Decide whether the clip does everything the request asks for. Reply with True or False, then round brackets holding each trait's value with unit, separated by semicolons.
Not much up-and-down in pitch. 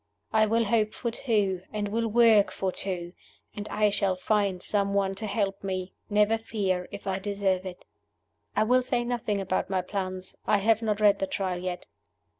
True (2.3 semitones)